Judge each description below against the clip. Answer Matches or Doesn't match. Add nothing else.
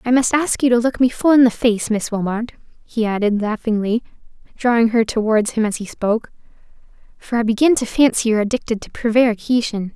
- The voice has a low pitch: Doesn't match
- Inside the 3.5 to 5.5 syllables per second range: Doesn't match